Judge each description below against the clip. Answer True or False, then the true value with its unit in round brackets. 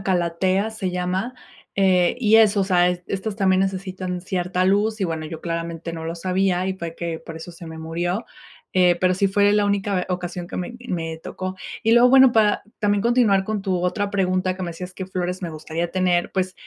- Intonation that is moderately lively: False (2.2 semitones)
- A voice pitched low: False (185 Hz)